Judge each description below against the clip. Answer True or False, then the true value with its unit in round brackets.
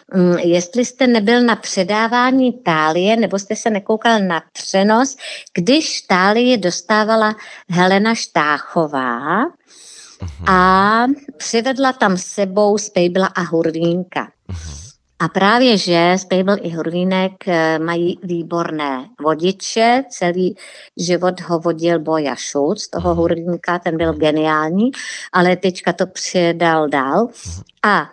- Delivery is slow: True (105 wpm)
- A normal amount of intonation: True (4.5 semitones)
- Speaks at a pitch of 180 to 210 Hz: True (185 Hz)